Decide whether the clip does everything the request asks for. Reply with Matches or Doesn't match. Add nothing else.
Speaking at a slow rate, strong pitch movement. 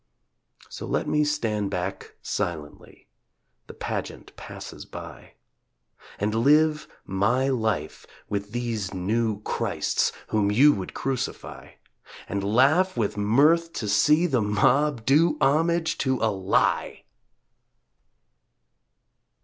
Matches